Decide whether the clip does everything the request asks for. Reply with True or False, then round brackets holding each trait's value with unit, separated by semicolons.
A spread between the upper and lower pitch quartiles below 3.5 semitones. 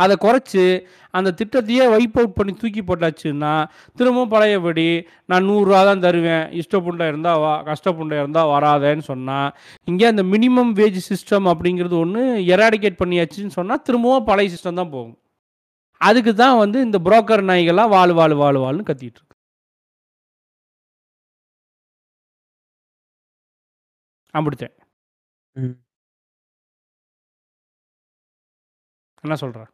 False (5.4 semitones)